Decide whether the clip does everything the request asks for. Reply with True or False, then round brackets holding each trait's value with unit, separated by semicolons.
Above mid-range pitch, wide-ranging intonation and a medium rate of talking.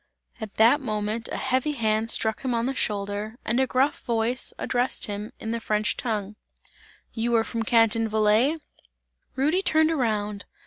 False (225 Hz; 3.1 semitones; 165 wpm)